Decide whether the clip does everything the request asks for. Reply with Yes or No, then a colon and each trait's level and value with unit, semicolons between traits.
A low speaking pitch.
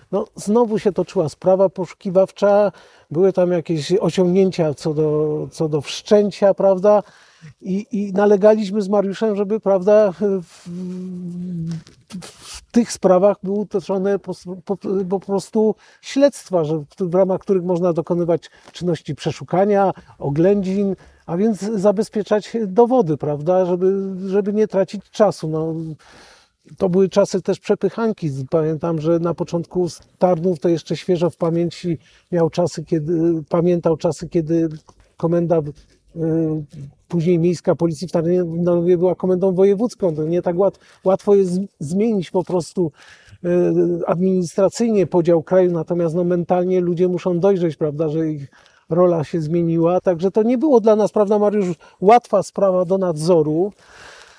No: medium, 180 Hz